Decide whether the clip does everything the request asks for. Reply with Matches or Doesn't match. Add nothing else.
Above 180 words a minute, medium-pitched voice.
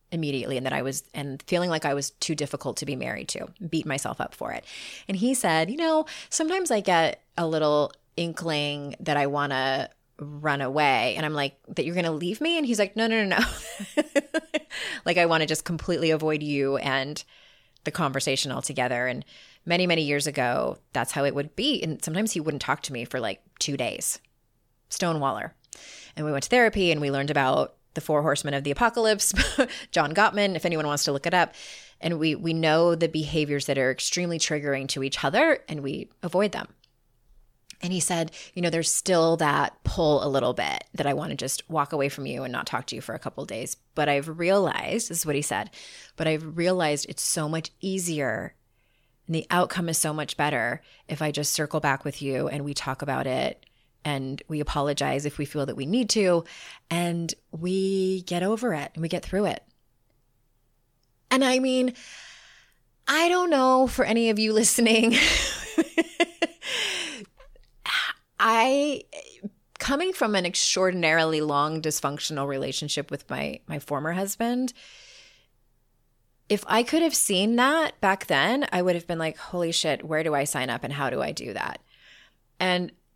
Matches